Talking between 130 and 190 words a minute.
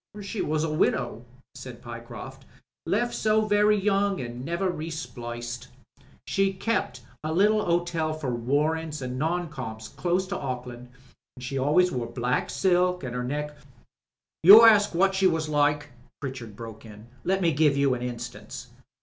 Yes: average, 165 wpm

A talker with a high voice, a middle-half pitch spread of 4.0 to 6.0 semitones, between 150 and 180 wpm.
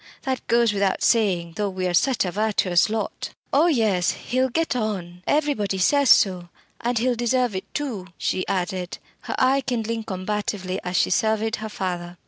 Yes: high, 210 Hz; average, 4.6 semitones; average, 170 wpm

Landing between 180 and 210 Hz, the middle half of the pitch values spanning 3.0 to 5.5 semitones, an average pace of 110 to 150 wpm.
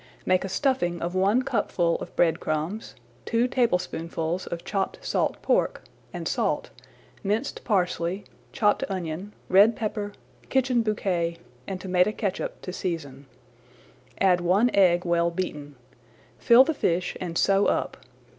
Yes: medium, 185 Hz; average, 3.6 semitones; average, 140 wpm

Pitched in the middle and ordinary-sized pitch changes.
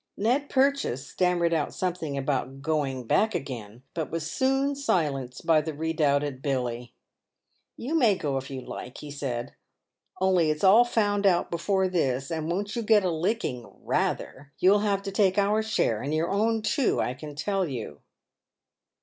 No: medium, 165 Hz; wide, 6.7 semitones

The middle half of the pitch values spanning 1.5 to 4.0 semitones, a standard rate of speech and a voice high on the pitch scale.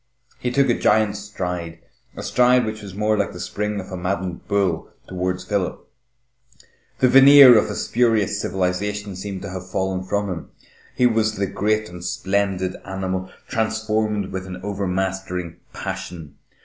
No: narrow, 2.6 semitones; average, 155 wpm; low, 100 Hz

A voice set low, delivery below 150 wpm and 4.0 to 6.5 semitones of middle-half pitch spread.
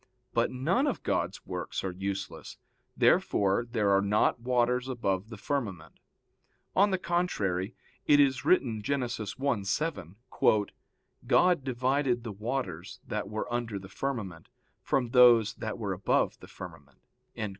Yes: low, 120 Hz; slow, 135 wpm; average, 5.1 semitones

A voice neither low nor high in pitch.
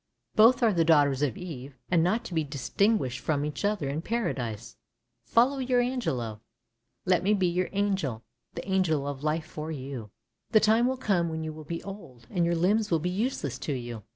Yes: medium, 165 Hz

